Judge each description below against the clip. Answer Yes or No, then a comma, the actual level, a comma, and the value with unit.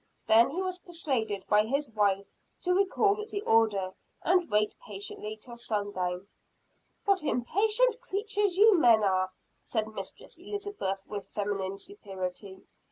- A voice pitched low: No, high, 225 Hz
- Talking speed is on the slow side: Yes, slow, 130 wpm